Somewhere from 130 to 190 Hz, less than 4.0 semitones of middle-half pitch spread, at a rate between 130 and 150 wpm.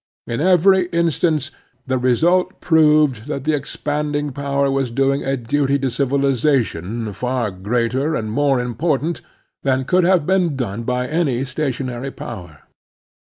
Yes: low, 135 Hz; average, 3.6 semitones; average, 140 wpm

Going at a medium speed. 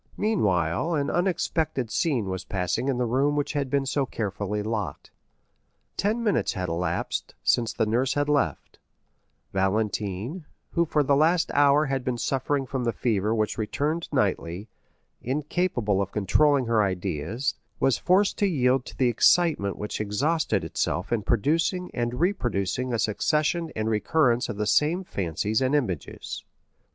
Yes: average, 150 wpm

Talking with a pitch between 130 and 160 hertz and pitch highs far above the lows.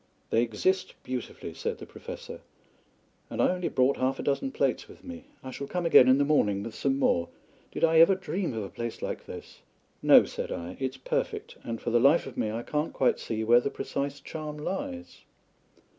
Yes: medium, 140 Hz; wide, 6.9 semitones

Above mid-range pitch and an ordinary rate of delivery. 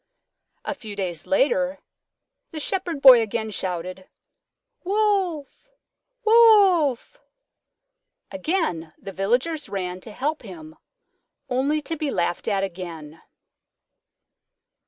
No: very high, 255 Hz; slow, 95 wpm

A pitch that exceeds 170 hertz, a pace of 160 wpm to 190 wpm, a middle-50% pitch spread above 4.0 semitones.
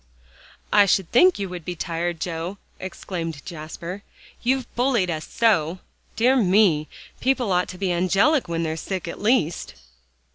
No: medium, 185 Hz; average, 150 wpm; average, 4.8 semitones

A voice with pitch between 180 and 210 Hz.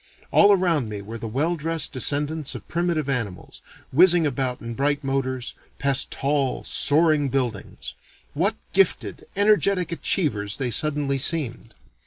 No: medium, 140 Hz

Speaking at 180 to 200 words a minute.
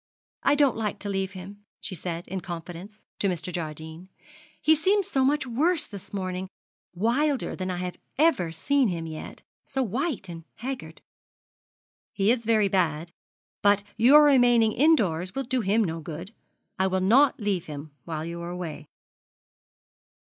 No: average, 160 wpm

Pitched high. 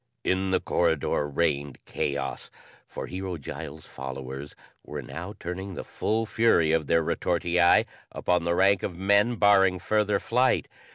No: very low, 90 Hz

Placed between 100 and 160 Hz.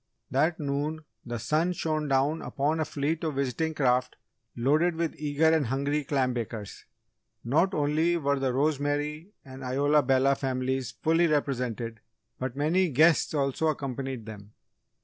Yes: medium, 140 Hz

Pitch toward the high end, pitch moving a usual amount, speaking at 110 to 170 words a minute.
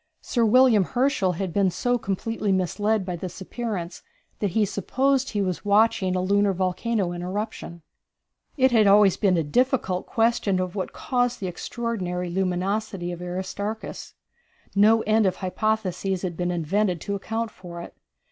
Yes: high, 200 Hz; average, 3.4 semitones; average, 155 wpm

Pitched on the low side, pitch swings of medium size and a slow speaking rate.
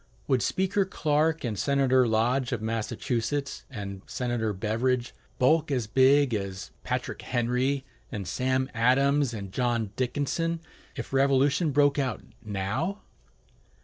Yes: low, 130 Hz; average, 3.8 semitones; slow, 120 wpm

